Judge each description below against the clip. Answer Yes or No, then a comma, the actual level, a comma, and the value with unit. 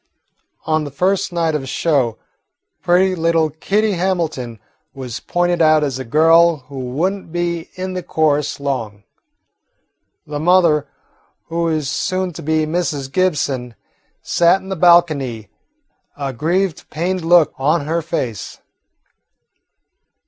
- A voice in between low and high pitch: Yes, medium, 160 Hz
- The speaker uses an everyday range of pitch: Yes, average, 3.7 semitones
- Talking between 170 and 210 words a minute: No, slow, 135 wpm